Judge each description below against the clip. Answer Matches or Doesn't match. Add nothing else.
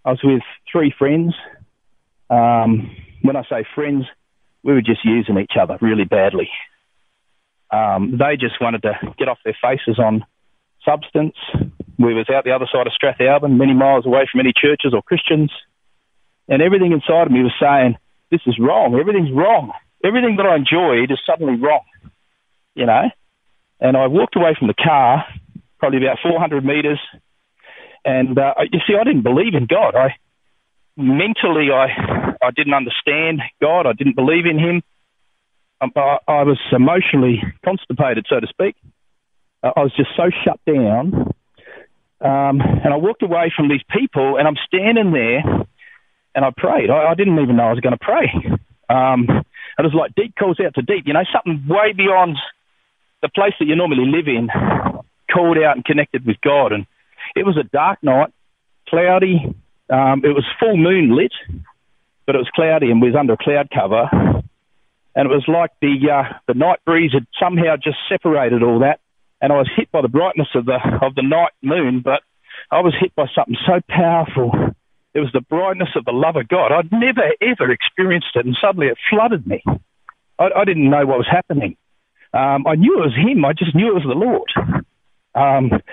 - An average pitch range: Matches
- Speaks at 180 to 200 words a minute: Matches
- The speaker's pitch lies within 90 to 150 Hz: Matches